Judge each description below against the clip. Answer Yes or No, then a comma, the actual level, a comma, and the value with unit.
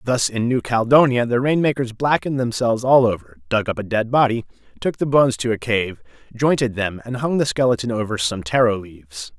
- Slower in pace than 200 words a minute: No, fast, 205 wpm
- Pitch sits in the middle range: No, low, 115 Hz